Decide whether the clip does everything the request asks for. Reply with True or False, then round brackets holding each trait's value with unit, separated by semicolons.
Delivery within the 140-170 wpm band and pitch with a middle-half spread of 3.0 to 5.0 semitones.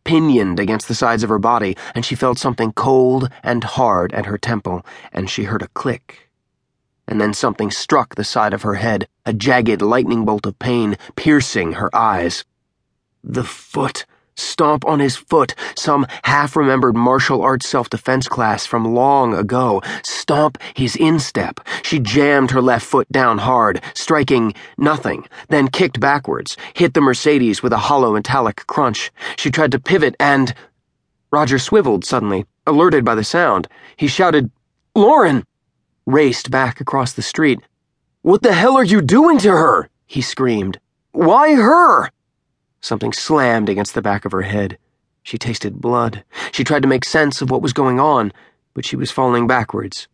True (165 wpm; 4.1 semitones)